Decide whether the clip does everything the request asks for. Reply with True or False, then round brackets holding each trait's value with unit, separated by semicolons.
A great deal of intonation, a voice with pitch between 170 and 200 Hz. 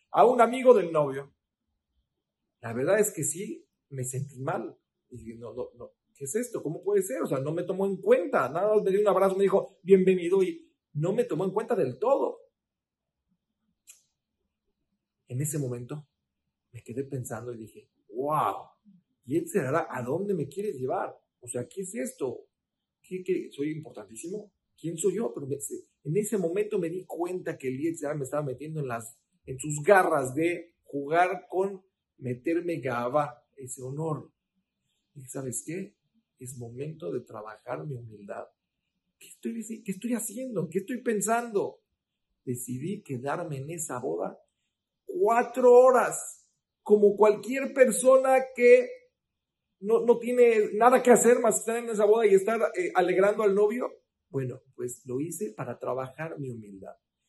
True (8.9 semitones; 185 Hz)